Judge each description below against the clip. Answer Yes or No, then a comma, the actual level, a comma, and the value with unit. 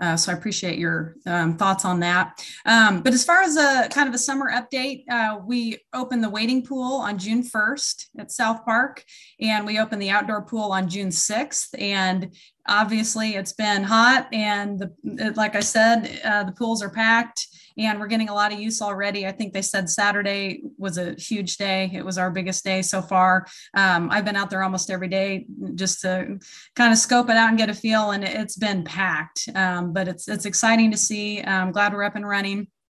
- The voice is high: Yes, high, 205 Hz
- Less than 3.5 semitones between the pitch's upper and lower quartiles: Yes, average, 2.9 semitones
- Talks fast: Yes, fast, 210 wpm